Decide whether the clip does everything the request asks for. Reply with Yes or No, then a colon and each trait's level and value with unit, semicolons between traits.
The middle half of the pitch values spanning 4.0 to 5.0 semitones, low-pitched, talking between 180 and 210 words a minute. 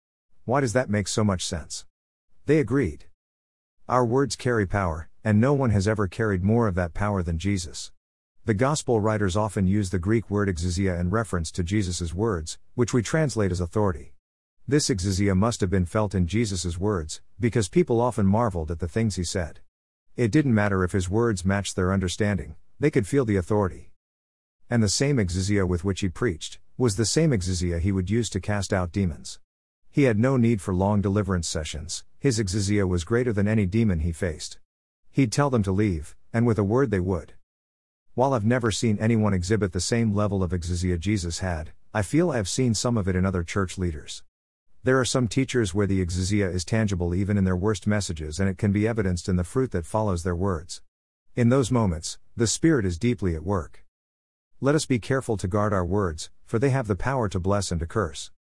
Yes: average, 4.3 semitones; low, 100 Hz; fast, 205 wpm